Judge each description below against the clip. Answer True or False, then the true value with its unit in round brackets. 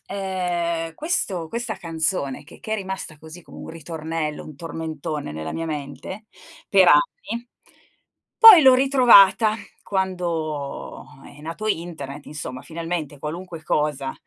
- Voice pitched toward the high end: False (165 Hz)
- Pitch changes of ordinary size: True (4.1 semitones)